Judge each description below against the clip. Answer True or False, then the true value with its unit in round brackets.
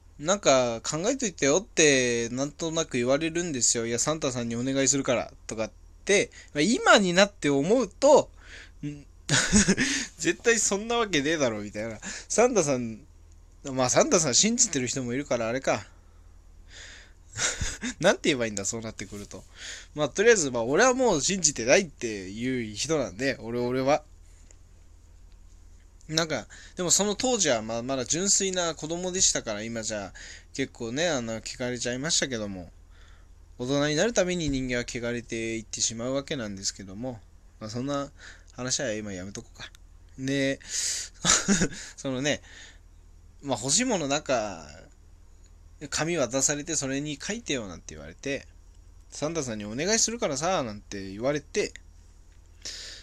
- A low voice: True (120 Hz)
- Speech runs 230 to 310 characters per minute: False (320 characters per minute)